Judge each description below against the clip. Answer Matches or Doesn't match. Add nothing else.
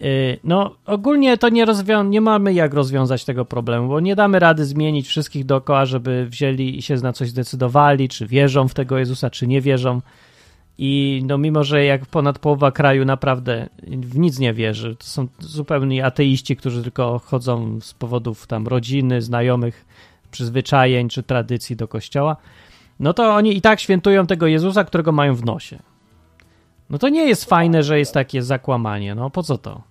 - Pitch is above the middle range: Doesn't match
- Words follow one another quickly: Matches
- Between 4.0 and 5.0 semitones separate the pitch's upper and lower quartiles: Doesn't match